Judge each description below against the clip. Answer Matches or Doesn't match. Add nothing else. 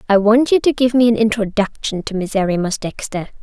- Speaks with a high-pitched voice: Matches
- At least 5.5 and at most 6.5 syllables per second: Matches